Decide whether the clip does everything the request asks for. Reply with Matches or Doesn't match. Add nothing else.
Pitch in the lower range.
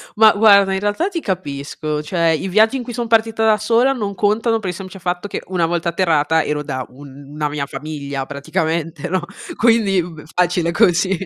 Doesn't match